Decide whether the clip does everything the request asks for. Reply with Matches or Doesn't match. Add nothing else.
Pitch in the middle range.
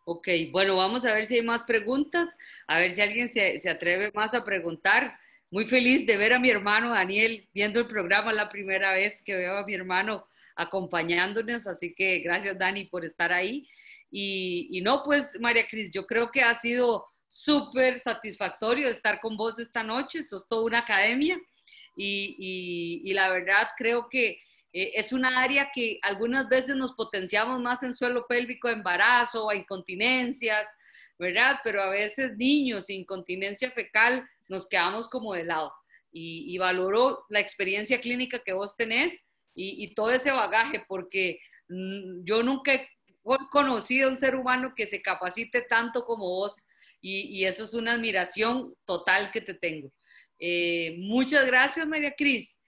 Doesn't match